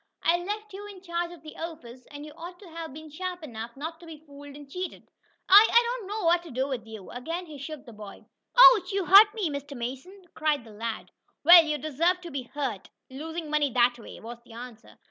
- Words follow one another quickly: Yes, fast, 225 wpm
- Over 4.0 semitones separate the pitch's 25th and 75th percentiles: Yes, average, 5.2 semitones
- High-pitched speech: Yes, very high, 310 Hz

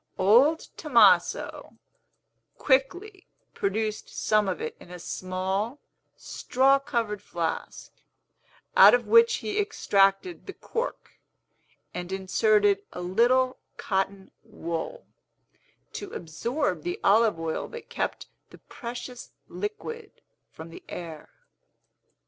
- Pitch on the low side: No, high, 215 Hz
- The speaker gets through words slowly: Yes, slow, 105 wpm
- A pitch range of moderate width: No, wide, 7.4 semitones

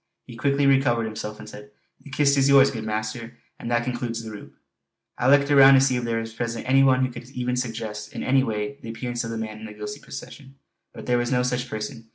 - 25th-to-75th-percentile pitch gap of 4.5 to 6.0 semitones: No, average, 3.1 semitones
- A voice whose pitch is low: Yes, low, 120 Hz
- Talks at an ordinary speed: No, fast, 245 wpm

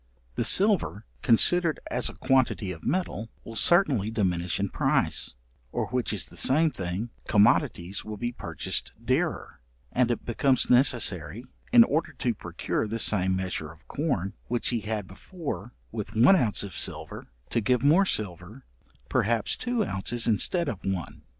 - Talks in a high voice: No, low, 115 Hz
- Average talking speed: Yes, average, 155 wpm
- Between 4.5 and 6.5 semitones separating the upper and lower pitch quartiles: Yes, wide, 5.4 semitones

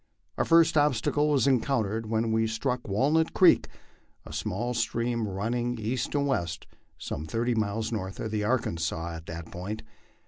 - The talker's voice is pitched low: Yes, low, 115 Hz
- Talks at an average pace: Yes, average, 165 wpm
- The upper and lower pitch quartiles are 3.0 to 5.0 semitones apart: Yes, average, 3.6 semitones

